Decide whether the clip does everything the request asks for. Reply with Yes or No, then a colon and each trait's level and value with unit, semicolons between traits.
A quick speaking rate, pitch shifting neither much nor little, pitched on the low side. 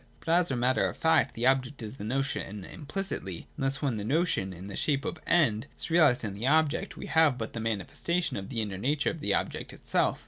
No: fast, 235 wpm; wide, 6.6 semitones; low, 130 Hz